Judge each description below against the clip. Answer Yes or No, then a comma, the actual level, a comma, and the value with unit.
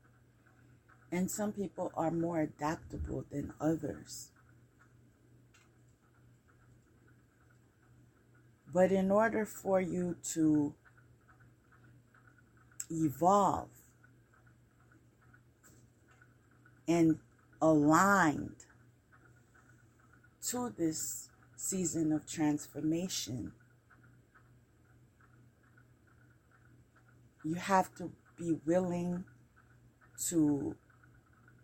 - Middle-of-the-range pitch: No, low, 120 Hz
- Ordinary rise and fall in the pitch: Yes, average, 4.7 semitones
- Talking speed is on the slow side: Yes, slow, 55 wpm